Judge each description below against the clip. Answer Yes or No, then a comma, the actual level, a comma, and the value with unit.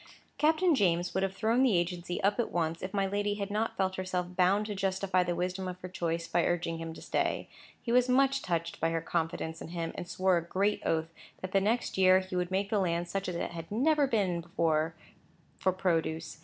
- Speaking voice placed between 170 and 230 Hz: Yes, medium, 185 Hz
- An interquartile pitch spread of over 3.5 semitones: No, average, 3.1 semitones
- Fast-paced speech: Yes, fast, 225 wpm